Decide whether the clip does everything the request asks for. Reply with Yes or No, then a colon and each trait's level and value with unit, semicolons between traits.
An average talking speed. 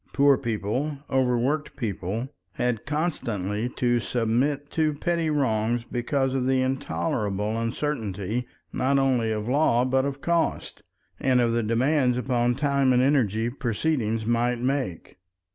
No: slow, 130 wpm